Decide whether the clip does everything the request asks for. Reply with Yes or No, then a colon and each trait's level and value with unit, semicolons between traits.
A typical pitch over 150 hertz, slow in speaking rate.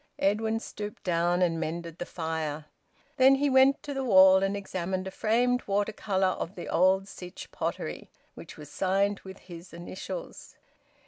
No: high, 190 Hz; average, 165 wpm